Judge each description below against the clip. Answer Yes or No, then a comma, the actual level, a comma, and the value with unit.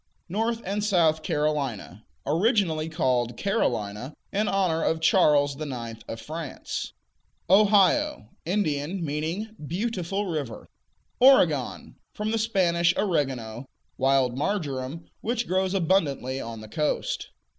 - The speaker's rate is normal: No, slow, 110 wpm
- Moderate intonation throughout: No, wide, 6.5 semitones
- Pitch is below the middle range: No, medium, 160 Hz